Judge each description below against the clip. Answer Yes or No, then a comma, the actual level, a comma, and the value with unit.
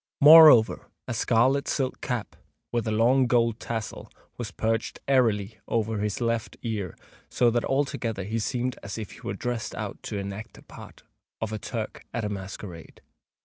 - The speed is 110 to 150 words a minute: No, average, 170 wpm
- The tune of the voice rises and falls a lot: No, average, 2.7 semitones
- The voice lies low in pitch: Yes, low, 115 Hz